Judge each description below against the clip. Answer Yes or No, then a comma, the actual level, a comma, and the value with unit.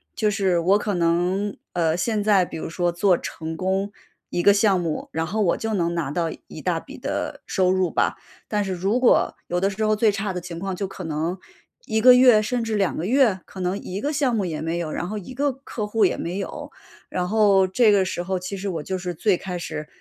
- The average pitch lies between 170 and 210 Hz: Yes, high, 190 Hz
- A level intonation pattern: No, average, 3.2 semitones